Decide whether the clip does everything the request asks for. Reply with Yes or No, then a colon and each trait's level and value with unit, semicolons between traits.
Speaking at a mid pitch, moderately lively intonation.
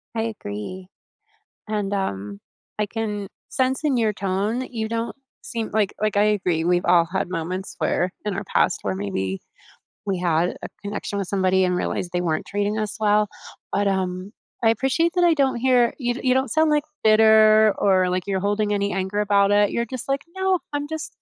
No: high, 205 Hz; average, 3.7 semitones